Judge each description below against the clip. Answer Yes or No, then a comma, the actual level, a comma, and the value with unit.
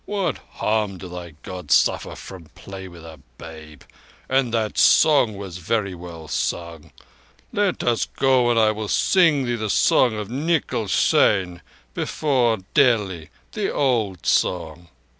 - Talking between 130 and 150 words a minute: Yes, average, 140 wpm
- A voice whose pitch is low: Yes, low, 105 Hz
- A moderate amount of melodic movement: No, wide, 6.0 semitones